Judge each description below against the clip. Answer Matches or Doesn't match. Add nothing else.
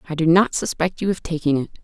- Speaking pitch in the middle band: Matches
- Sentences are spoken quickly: Matches